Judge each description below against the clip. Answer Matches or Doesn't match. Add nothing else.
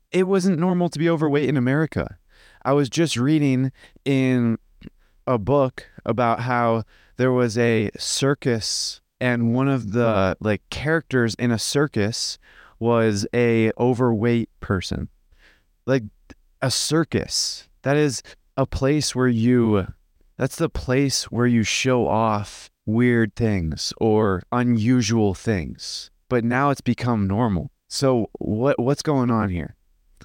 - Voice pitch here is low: Matches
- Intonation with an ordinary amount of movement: Matches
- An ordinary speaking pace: Doesn't match